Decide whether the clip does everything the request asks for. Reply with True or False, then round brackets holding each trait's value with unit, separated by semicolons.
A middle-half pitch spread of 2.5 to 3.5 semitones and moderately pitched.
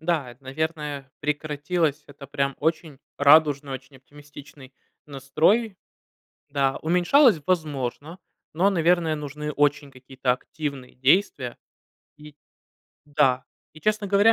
True (2.9 semitones; 145 Hz)